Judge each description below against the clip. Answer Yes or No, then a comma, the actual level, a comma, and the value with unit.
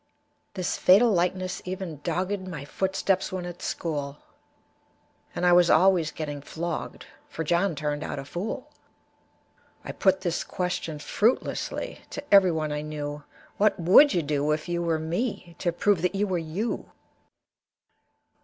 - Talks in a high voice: No, medium, 175 Hz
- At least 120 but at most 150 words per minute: Yes, average, 145 wpm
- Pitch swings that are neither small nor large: Yes, average, 3.4 semitones